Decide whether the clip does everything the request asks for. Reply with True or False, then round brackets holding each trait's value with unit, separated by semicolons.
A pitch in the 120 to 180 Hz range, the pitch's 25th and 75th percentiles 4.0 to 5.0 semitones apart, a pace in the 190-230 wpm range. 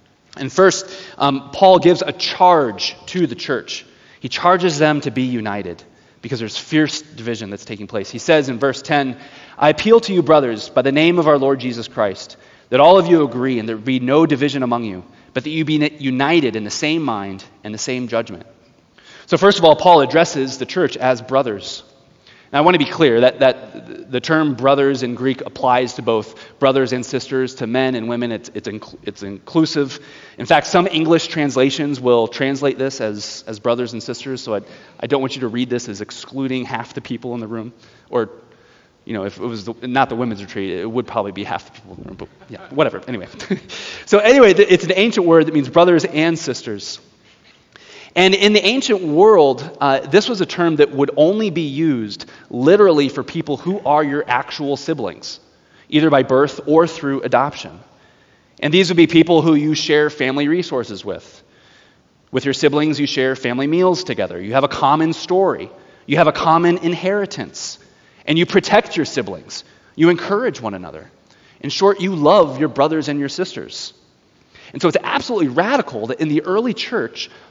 True (140 Hz; 4.7 semitones; 200 wpm)